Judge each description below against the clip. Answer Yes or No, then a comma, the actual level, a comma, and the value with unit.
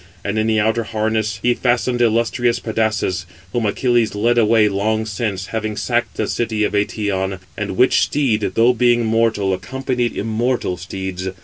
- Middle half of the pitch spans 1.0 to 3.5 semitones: Yes, narrow, 2.4 semitones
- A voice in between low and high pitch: No, low, 110 Hz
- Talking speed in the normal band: Yes, average, 155 wpm